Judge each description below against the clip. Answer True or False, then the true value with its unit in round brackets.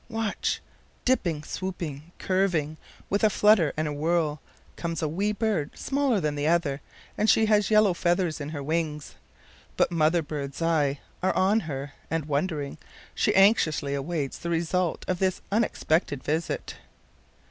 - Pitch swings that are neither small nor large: True (4.3 semitones)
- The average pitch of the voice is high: False (165 Hz)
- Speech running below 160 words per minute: True (150 wpm)